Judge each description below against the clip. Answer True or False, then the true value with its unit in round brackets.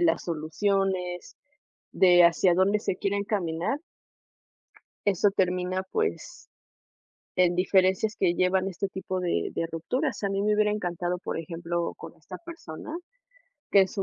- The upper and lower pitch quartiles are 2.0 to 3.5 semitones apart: True (2.4 semitones)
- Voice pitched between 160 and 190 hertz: True (185 Hz)